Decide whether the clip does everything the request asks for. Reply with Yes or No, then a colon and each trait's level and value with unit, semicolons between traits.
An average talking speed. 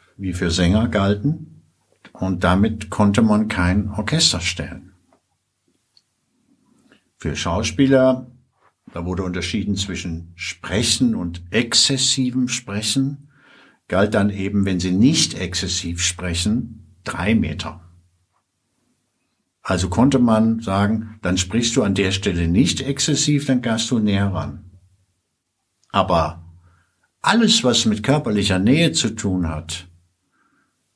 No: slow, 110 wpm